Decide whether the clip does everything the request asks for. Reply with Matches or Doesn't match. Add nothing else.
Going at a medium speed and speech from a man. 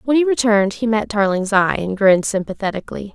Doesn't match